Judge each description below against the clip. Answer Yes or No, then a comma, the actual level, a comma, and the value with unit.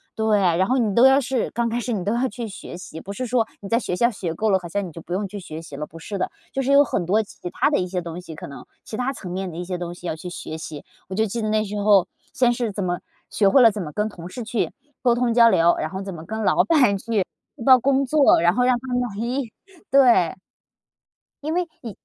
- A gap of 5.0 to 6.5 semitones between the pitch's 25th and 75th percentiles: Yes, average, 5.3 semitones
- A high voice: Yes, high, 210 Hz